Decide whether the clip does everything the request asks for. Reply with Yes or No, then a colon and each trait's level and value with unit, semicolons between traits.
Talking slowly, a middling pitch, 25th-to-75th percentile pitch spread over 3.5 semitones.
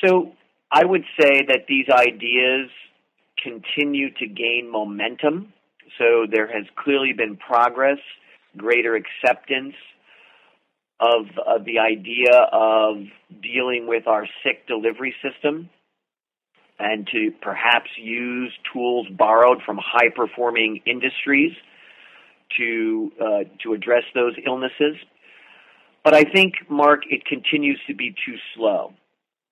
No: slow, 115 wpm; low, 125 Hz; average, 4.0 semitones